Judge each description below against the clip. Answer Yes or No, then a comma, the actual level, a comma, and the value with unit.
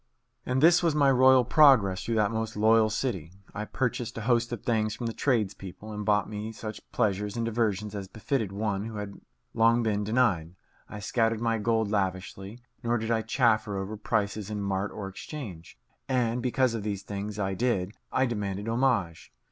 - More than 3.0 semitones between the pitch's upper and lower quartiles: No, average, 2.7 semitones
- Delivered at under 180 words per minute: No, average, 185 wpm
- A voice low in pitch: Yes, low, 110 Hz